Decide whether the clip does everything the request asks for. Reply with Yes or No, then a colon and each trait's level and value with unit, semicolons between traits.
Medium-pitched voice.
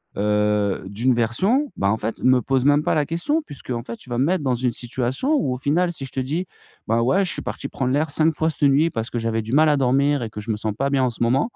No: low, 130 Hz